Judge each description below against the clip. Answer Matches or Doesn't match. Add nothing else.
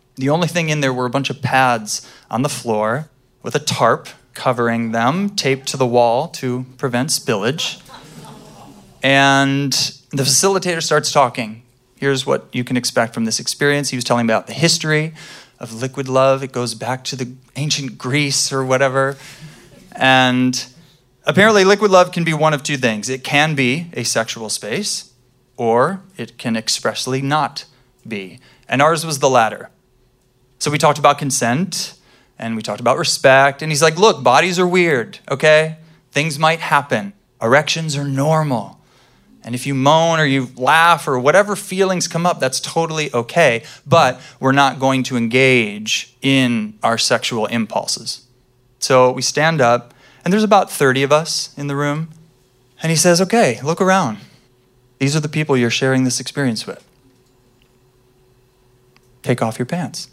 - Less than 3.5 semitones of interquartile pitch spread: Doesn't match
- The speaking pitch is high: Doesn't match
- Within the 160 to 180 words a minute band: Matches